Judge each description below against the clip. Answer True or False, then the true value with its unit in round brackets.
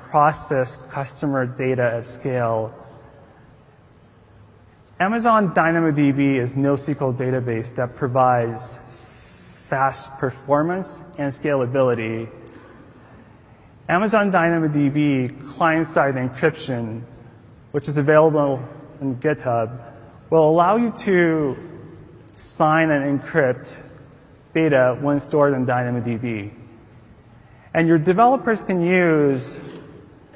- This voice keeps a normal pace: False (85 wpm)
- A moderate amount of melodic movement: True (4.1 semitones)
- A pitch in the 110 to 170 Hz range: True (135 Hz)